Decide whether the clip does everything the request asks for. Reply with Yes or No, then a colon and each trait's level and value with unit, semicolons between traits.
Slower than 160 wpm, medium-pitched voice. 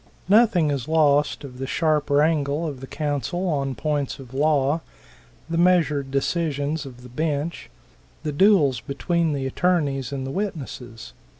Yes: average, 145 wpm; medium, 145 Hz